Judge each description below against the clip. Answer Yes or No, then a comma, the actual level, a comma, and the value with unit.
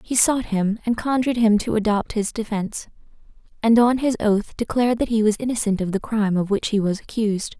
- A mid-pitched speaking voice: No, high, 220 Hz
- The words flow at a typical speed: No, fast, 215 wpm